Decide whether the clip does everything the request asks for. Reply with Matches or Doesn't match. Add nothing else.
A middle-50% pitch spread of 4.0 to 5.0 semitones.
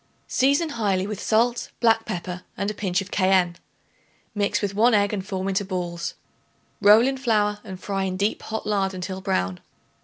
Doesn't match